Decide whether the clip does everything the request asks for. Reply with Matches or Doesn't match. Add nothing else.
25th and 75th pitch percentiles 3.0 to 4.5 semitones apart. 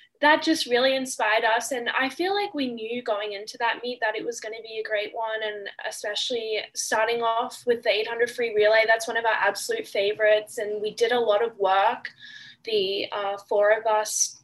Doesn't match